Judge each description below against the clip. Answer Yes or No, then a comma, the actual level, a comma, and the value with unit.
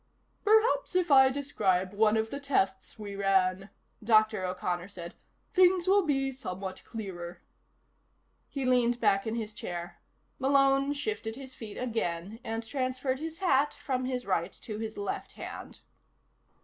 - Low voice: No, high, 225 Hz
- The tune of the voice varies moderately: No, wide, 5.7 semitones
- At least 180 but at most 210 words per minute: No, average, 145 wpm